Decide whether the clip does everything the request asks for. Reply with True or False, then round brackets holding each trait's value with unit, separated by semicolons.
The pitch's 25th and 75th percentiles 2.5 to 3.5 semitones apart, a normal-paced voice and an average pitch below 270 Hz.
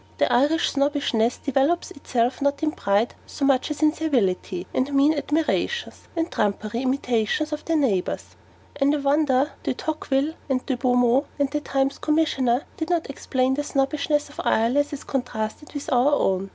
False (3.2 semitones; 165 wpm; 275 Hz)